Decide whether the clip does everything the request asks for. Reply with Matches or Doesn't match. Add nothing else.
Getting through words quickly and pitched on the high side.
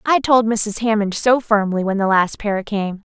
Matches